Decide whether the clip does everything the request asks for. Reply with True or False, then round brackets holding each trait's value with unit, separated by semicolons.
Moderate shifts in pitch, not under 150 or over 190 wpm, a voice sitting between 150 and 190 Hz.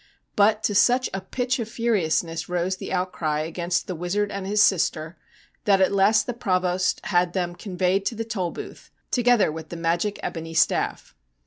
True (3.4 semitones; 180 wpm; 185 Hz)